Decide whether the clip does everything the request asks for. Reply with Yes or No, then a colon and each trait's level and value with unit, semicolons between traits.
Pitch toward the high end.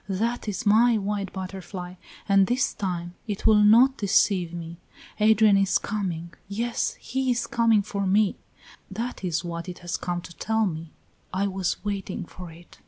Yes: high, 195 Hz